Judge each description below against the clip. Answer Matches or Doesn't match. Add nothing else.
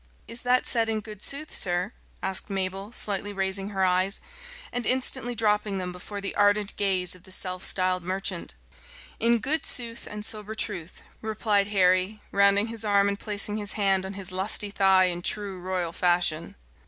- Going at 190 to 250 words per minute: Doesn't match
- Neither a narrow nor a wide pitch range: Doesn't match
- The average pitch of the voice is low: Doesn't match